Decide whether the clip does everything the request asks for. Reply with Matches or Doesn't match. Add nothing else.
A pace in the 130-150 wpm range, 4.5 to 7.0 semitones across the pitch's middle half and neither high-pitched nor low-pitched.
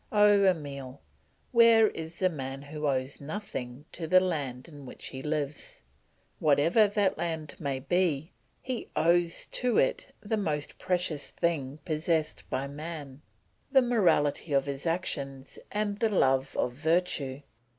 Matches